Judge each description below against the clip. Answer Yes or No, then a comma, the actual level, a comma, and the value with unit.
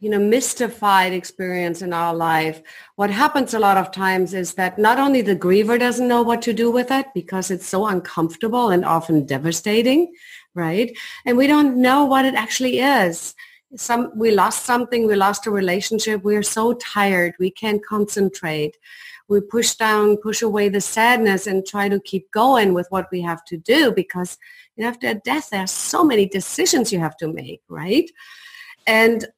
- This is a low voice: No, high, 210 Hz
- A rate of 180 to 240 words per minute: Yes, average, 185 wpm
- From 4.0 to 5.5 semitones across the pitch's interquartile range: Yes, average, 4.6 semitones